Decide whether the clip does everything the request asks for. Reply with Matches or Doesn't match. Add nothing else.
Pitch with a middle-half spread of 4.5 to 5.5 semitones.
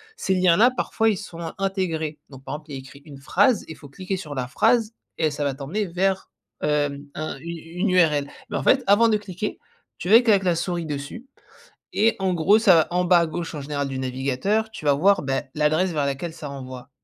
Matches